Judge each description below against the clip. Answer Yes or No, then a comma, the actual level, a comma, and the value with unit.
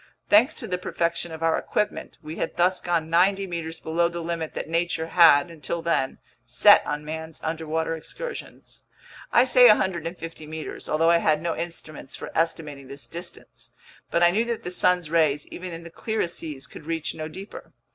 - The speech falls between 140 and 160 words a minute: No, average, 185 wpm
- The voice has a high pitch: No, medium, 165 Hz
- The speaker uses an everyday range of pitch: No, narrow, 1.8 semitones